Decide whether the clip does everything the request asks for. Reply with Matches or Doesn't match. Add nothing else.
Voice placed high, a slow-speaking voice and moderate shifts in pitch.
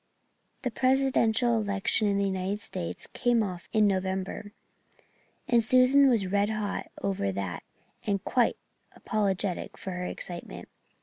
Matches